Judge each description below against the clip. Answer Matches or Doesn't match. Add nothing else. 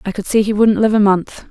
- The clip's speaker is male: Doesn't match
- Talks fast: Matches